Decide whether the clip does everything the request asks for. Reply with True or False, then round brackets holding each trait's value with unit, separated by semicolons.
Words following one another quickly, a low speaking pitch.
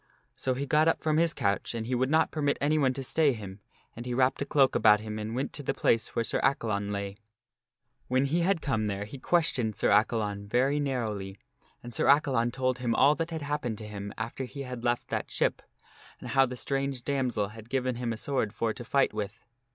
True (225 wpm; 125 Hz)